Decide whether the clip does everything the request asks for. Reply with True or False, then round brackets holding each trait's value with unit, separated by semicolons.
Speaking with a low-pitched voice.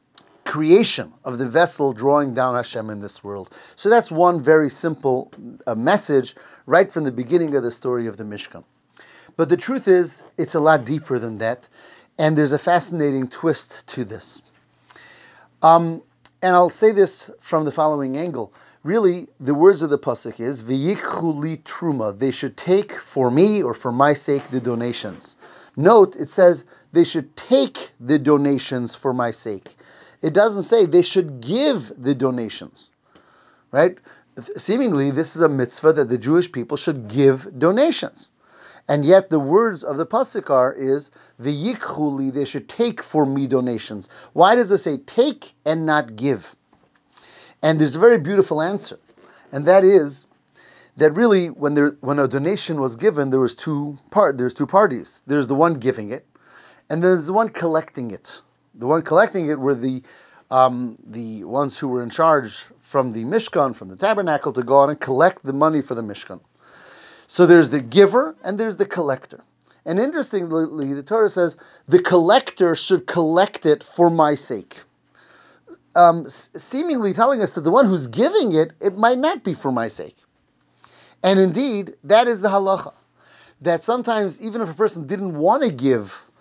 False (155 Hz)